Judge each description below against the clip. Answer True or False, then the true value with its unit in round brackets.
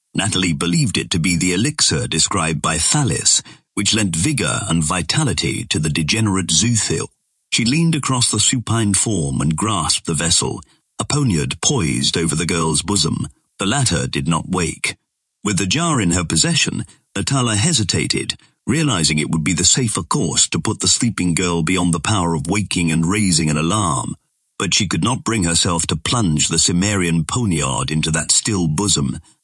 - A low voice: True (90 Hz)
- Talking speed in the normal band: True (175 wpm)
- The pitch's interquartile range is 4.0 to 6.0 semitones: True (4.6 semitones)